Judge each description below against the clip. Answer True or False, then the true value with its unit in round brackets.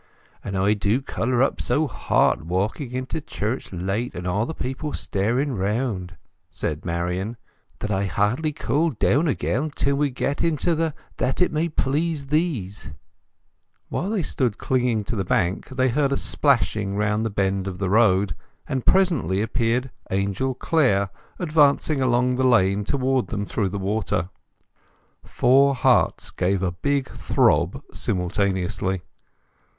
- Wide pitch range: True (6.0 semitones)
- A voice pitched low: True (115 Hz)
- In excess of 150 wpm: False (145 wpm)